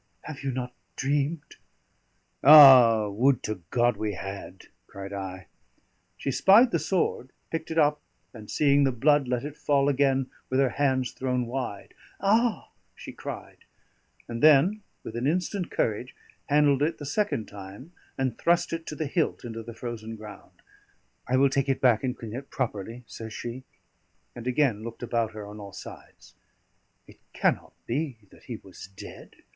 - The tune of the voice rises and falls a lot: No, average, 4.3 semitones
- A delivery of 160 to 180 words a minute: Yes, average, 165 wpm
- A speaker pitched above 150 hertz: No, low, 130 Hz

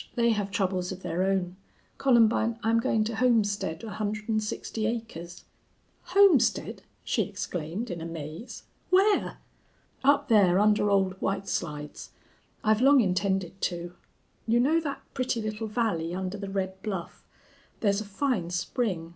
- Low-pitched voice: No, high, 205 Hz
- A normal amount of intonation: Yes, average, 3.9 semitones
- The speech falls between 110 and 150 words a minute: Yes, average, 145 wpm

